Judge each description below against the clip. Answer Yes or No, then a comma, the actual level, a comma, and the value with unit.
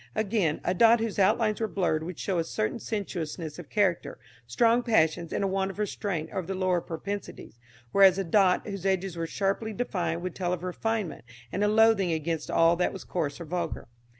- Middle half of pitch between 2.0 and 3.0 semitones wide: No, average, 3.5 semitones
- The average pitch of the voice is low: No, medium, 185 Hz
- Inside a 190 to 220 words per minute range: Yes, average, 200 wpm